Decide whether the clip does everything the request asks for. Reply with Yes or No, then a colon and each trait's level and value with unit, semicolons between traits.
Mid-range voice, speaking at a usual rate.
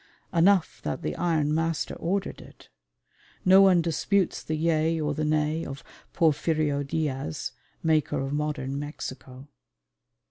No: medium, 155 Hz; slow, 130 wpm